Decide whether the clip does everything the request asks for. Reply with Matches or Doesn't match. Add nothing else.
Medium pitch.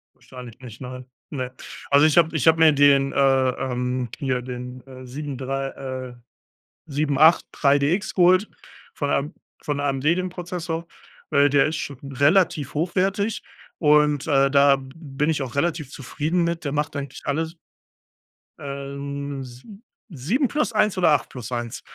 Matches